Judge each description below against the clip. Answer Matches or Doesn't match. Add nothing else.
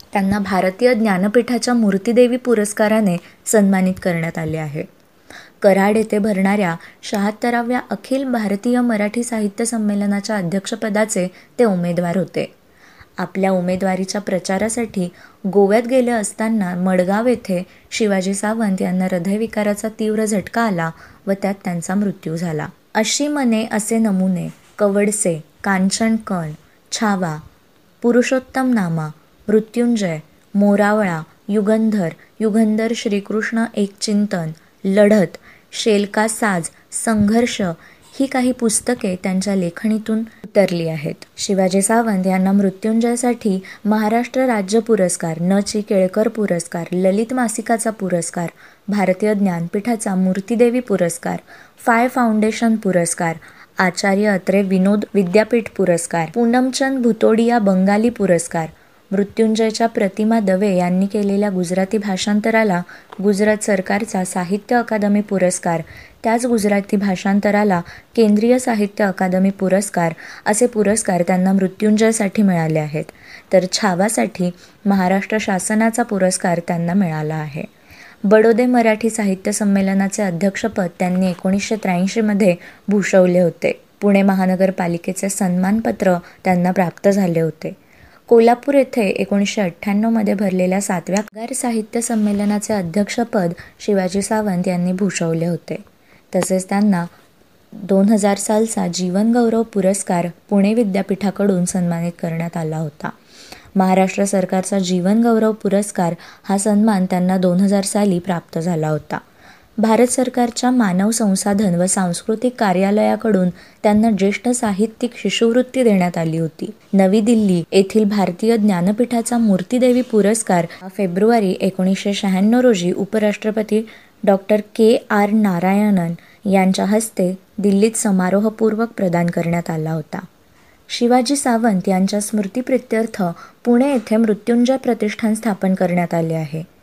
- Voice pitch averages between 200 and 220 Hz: Matches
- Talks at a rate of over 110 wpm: Doesn't match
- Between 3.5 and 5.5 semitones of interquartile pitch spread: Doesn't match